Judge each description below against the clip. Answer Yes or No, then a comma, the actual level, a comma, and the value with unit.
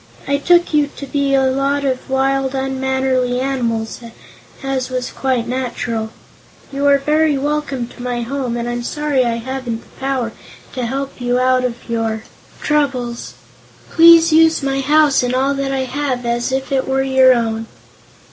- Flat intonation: Yes, narrow, 2.1 semitones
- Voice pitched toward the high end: Yes, very high, 265 Hz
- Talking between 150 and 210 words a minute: Yes, average, 165 wpm